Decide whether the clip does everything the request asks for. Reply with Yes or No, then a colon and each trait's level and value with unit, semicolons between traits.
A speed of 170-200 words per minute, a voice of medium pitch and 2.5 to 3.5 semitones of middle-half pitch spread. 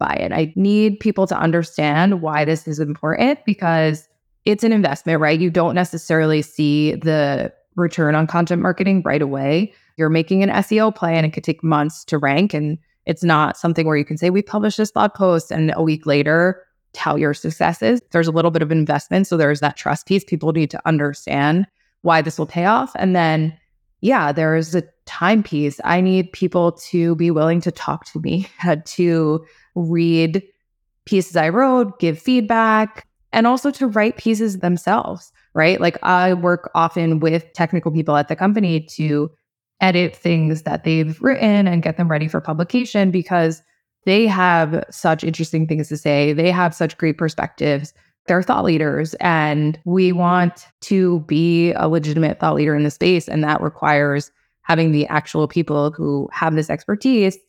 Yes: average, 175 wpm; medium, 165 Hz; average, 3.0 semitones